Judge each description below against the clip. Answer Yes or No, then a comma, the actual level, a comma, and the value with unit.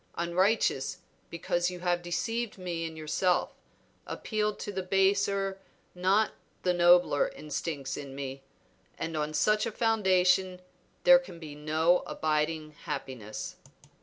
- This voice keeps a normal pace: No, slow, 125 wpm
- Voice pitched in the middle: Yes, medium, 175 Hz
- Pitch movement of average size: Yes, average, 3.9 semitones